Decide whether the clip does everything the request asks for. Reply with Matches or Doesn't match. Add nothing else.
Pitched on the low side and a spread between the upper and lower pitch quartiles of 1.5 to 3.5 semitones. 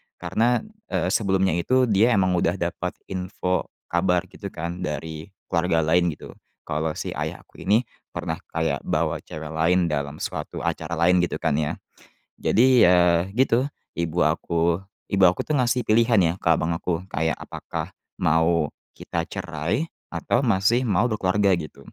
Doesn't match